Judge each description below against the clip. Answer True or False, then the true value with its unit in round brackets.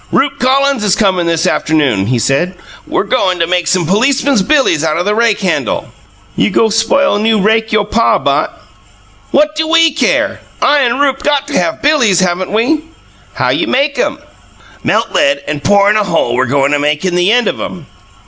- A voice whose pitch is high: True (210 Hz)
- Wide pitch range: True (7.7 semitones)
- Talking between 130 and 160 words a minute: False (200 wpm)